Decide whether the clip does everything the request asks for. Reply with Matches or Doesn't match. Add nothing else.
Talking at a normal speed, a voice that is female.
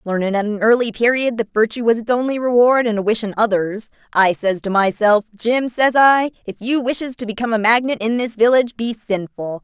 Doesn't match